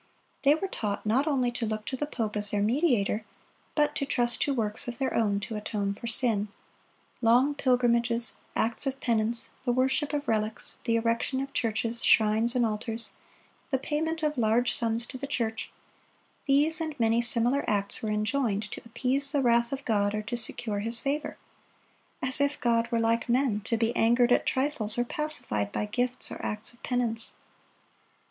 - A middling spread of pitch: Yes, average, 3.3 semitones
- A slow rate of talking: No, average, 180 wpm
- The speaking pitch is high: Yes, high, 235 Hz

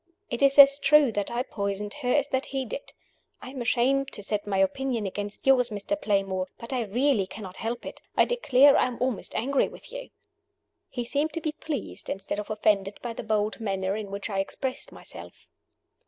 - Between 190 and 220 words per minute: Yes, average, 200 wpm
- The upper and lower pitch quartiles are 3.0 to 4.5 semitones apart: No, average, 5.1 semitones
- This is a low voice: No, high, 235 Hz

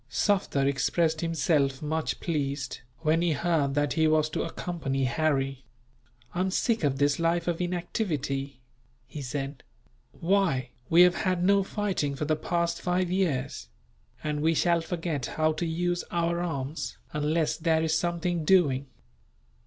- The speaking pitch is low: No, medium, 160 Hz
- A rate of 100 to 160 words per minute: Yes, average, 150 wpm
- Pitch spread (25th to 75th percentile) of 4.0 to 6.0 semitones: No, average, 3.5 semitones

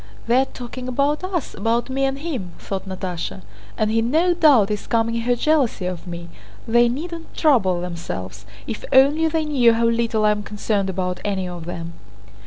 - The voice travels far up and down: Yes, wide, 6.4 semitones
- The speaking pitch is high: Yes, high, 230 Hz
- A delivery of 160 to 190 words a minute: Yes, average, 185 wpm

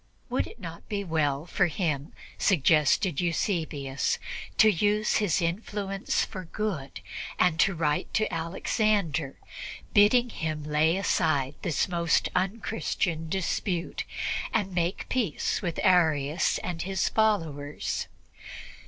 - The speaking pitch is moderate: Yes, medium, 175 Hz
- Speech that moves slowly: Yes, slow, 115 wpm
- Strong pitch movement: No, average, 4.2 semitones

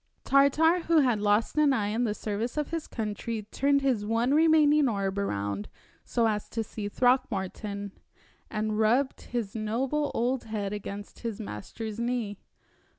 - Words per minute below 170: Yes, average, 155 wpm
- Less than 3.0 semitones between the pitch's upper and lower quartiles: No, average, 4.4 semitones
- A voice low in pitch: No, high, 225 Hz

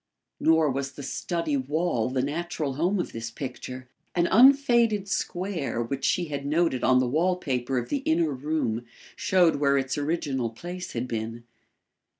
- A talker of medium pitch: Yes, medium, 145 Hz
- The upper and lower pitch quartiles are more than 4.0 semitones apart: Yes, average, 5.2 semitones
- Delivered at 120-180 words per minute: Yes, average, 160 wpm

